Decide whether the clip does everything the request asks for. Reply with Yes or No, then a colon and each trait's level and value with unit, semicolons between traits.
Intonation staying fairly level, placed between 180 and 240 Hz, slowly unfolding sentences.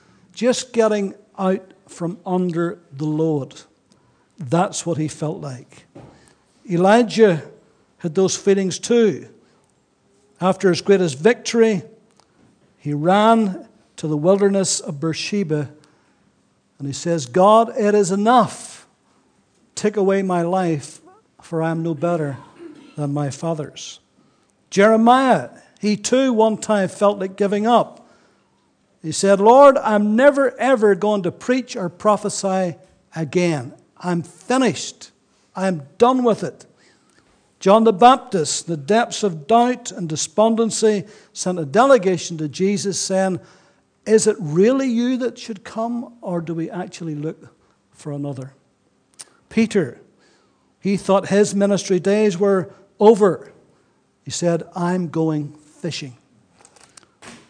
No: average, 4.8 semitones; high, 190 Hz; slow, 120 wpm